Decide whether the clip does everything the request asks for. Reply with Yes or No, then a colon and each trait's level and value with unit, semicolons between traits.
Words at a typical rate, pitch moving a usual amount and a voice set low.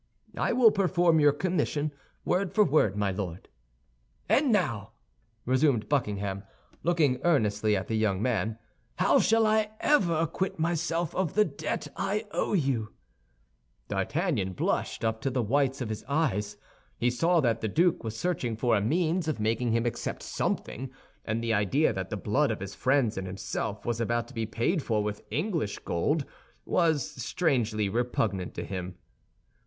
No: average, 165 wpm; wide, 7.4 semitones; low, 125 Hz